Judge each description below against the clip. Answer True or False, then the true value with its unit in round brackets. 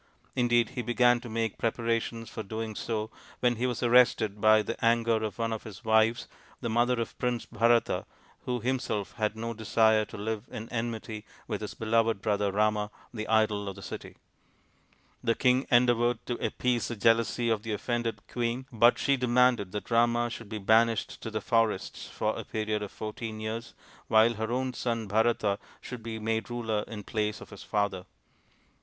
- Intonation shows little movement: True (1.7 semitones)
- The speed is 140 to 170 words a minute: False (185 wpm)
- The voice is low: True (115 Hz)